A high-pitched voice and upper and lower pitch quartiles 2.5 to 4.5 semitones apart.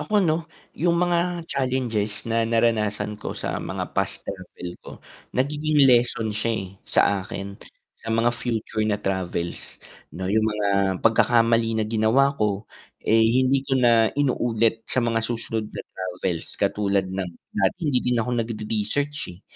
No: low, 115 Hz; average, 3.4 semitones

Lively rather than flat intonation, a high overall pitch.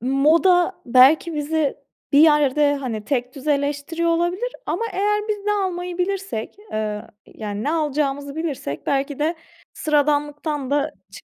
No: average, 3.9 semitones; very high, 295 Hz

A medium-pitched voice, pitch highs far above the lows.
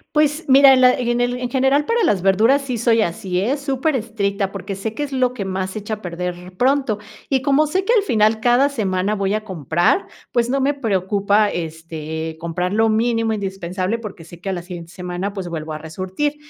No: high, 215 Hz; wide, 5.8 semitones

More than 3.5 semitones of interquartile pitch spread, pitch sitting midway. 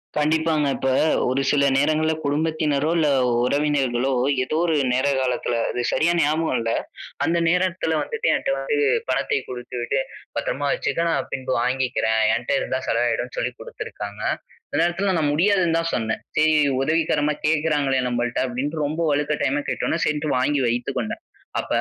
Yes: average, 3.9 semitones; medium, 145 Hz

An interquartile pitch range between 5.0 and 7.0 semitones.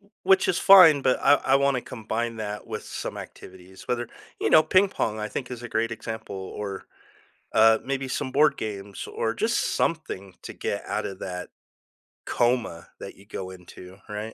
Yes: wide, 5.6 semitones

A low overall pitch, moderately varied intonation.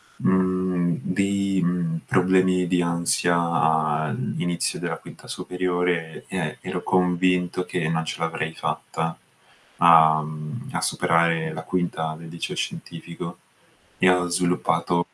No: very low, 85 Hz; narrow, 1.8 semitones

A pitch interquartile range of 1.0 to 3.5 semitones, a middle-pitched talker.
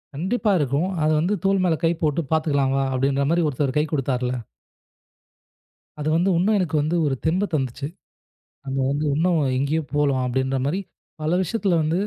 No: average, 3.9 semitones; medium, 150 Hz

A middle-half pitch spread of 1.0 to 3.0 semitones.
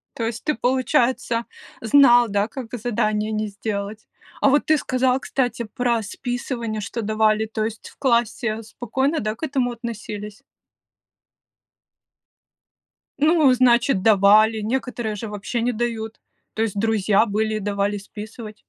Yes: narrow, 2.5 semitones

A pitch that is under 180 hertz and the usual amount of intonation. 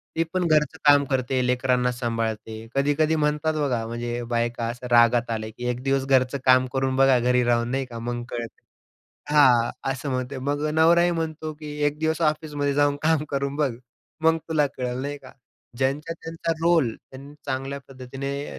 Yes: low, 135 Hz; average, 3.3 semitones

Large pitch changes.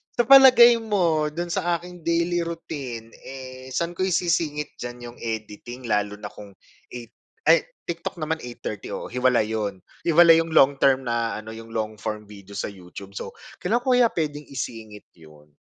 Yes: wide, 7.4 semitones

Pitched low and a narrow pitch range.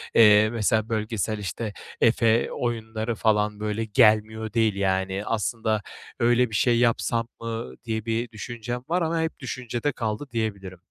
Yes: low, 110 Hz; narrow, 1.9 semitones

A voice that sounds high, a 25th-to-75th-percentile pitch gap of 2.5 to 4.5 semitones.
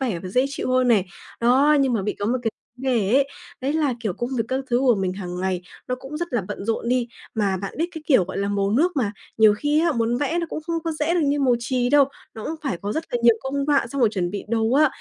No: high, 245 Hz; average, 5.1 semitones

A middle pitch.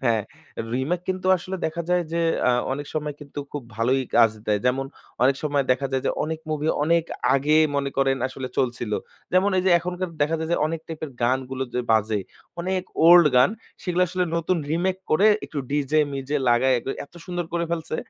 Yes: medium, 150 Hz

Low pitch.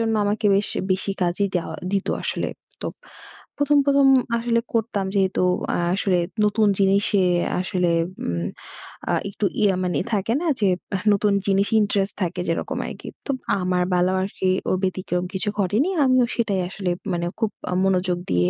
No: high, 195 Hz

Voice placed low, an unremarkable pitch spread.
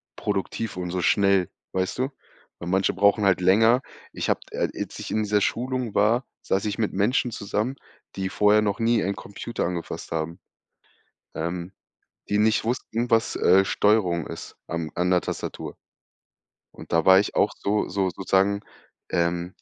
Yes: low, 100 Hz; average, 3.1 semitones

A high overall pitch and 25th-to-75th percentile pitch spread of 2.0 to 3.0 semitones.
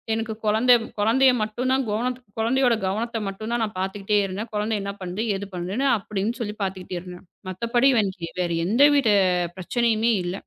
No: high, 215 Hz; average, 3.4 semitones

